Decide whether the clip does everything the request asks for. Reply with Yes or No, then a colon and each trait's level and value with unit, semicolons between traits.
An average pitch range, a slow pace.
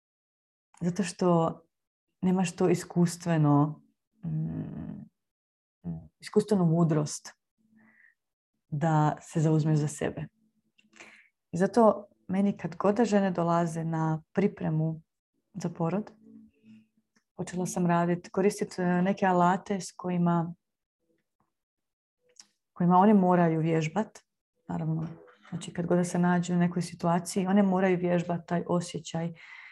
Yes: average, 3.3 semitones; slow, 100 wpm